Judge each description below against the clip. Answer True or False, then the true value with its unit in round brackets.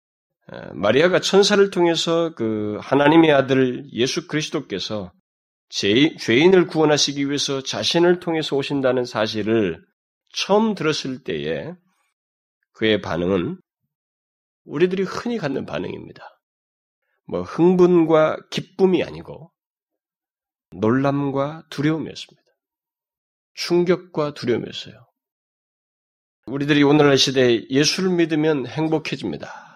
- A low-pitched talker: False (150 Hz)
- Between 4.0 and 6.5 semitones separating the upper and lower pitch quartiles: True (5.4 semitones)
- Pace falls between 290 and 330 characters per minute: False (255 characters per minute)